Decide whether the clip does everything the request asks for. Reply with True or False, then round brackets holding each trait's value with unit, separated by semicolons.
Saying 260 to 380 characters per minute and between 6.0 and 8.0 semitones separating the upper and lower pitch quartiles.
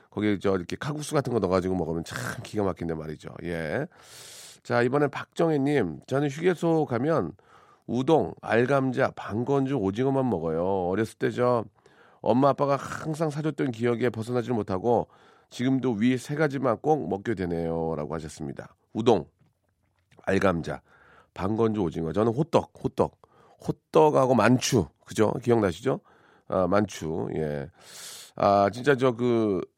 True (290 characters per minute; 6.4 semitones)